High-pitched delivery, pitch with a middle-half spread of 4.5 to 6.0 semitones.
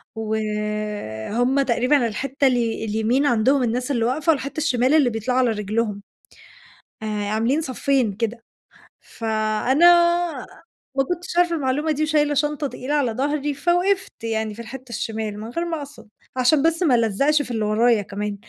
Yes: high, 245 Hz; average, 4.8 semitones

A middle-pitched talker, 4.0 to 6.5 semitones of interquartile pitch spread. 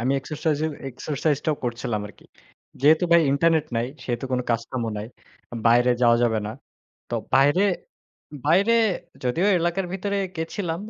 Yes: medium, 145 Hz; wide, 5.5 semitones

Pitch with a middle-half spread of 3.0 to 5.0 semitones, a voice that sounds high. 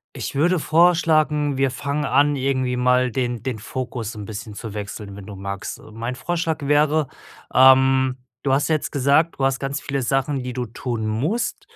No: average, 3.5 semitones; low, 130 Hz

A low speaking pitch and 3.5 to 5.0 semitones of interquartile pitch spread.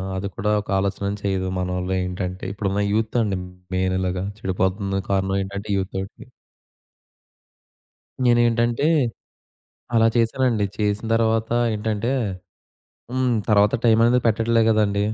No: low, 105 Hz; average, 2.9 semitones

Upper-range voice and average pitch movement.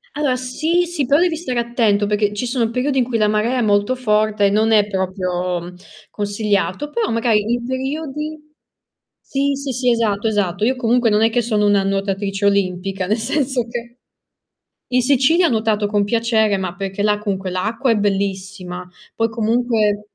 Yes: high, 220 Hz; average, 3.8 semitones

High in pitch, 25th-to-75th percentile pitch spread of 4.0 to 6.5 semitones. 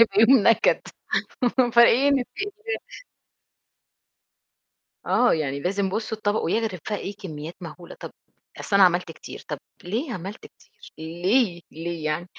Yes: high, 195 Hz; average, 5.1 semitones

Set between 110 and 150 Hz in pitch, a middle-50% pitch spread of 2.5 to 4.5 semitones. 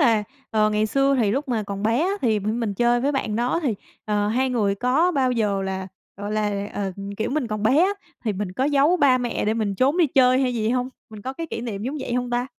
No: high, 235 Hz; average, 3.9 semitones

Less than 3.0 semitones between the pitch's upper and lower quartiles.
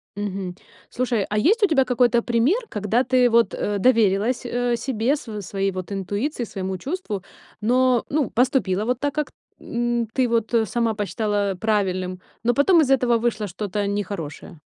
No: average, 3.7 semitones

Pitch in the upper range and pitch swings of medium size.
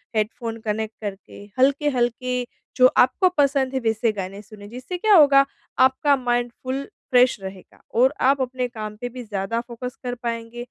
Yes: high, 245 Hz; average, 3.0 semitones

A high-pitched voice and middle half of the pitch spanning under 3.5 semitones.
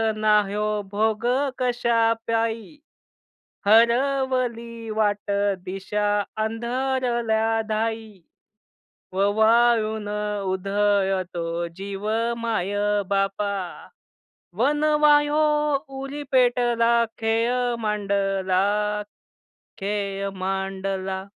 Yes: high, 220 Hz; average, 3.0 semitones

